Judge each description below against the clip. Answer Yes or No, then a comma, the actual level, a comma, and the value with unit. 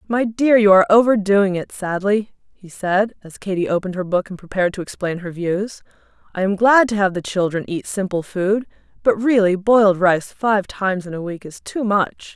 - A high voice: Yes, high, 195 Hz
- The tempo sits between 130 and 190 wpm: No, average, 200 wpm